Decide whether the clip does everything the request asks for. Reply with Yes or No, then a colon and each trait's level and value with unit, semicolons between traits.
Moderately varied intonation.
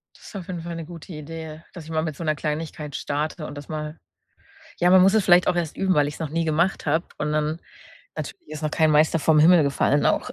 No: narrow, 2.0 semitones